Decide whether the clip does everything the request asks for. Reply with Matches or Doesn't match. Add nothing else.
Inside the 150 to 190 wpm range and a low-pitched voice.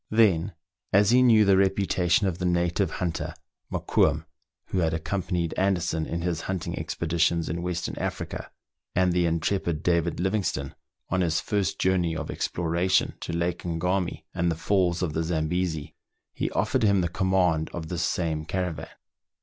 Matches